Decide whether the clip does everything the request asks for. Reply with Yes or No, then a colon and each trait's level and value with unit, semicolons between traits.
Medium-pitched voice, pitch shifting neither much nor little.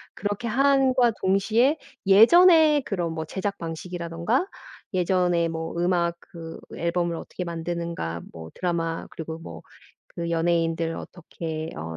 Yes: medium, 170 Hz; average, 3.6 semitones